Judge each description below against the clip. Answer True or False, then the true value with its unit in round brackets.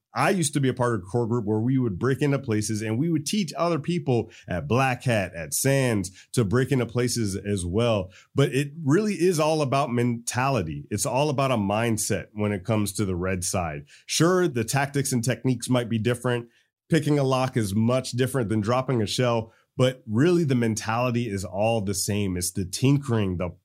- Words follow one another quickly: True (210 wpm)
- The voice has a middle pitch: False (120 Hz)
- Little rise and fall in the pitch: False (4.1 semitones)